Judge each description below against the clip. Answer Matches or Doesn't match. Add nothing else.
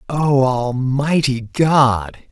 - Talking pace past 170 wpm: Doesn't match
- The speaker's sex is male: Matches